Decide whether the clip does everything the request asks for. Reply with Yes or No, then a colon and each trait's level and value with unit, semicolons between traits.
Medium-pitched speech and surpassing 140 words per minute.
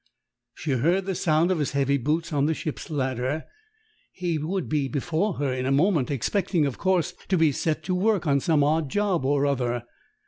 Yes: medium, 155 Hz; average, 200 wpm